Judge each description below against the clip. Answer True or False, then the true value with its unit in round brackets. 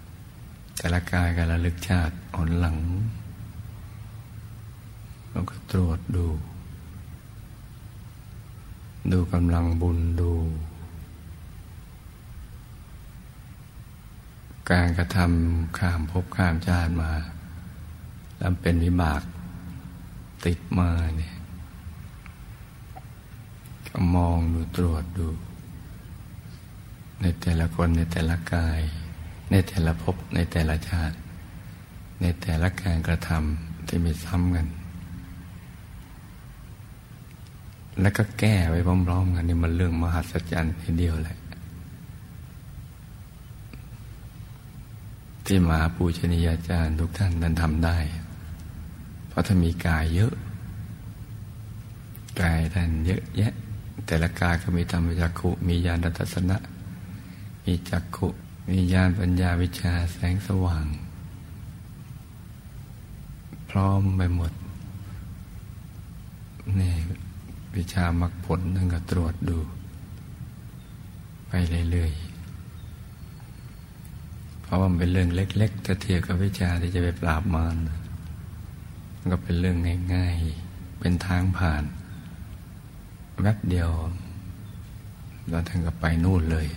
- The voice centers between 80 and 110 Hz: True (90 Hz)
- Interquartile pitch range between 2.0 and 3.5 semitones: True (2.5 semitones)